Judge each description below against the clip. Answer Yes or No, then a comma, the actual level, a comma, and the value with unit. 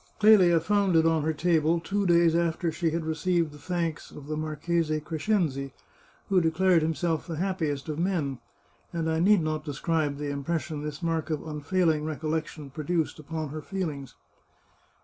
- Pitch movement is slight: Yes, narrow, 2.1 semitones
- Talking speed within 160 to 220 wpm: Yes, average, 170 wpm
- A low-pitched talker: No, medium, 160 Hz